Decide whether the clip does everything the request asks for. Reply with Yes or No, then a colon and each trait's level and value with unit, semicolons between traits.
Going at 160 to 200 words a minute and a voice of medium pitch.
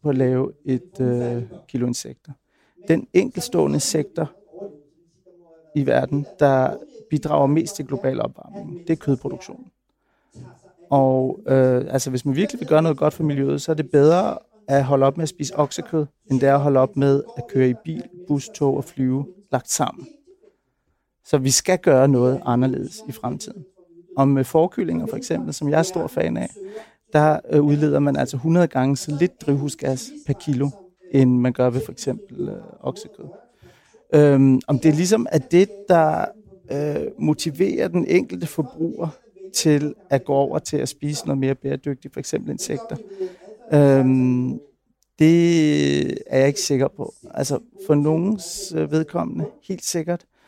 Yes: average, 165 wpm; medium, 150 Hz